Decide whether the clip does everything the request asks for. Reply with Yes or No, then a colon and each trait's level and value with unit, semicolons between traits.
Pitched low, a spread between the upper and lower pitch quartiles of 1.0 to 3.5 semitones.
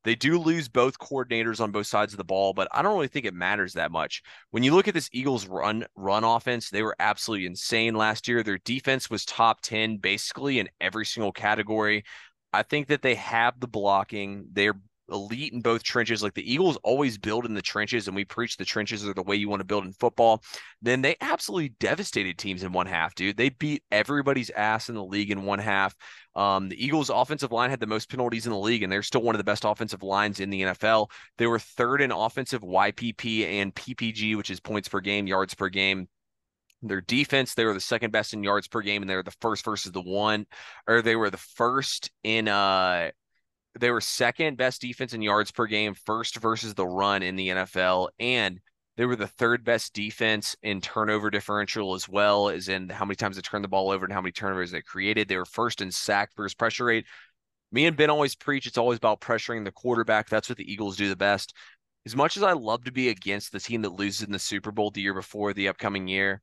Yes: low, 105 Hz; average, 2.9 semitones